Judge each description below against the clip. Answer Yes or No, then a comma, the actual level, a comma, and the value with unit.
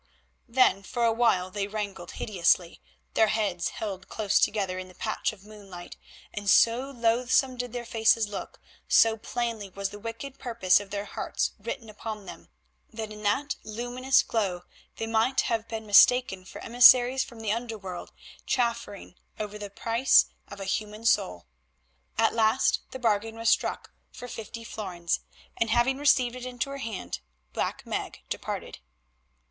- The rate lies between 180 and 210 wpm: No, average, 165 wpm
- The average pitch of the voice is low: No, high, 220 Hz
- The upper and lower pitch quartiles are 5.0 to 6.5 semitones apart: No, average, 2.9 semitones